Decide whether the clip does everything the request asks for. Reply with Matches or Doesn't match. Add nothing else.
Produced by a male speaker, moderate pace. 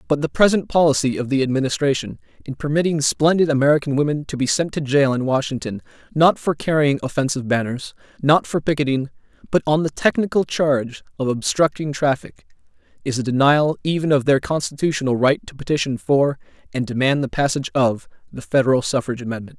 Matches